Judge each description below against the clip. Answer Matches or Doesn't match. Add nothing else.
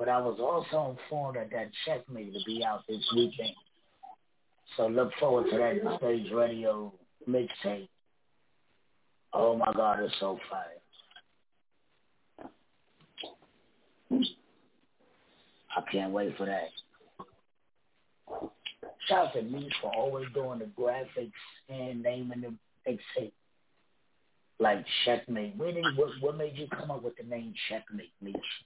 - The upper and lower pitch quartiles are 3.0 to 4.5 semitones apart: Matches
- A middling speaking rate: Doesn't match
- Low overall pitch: Matches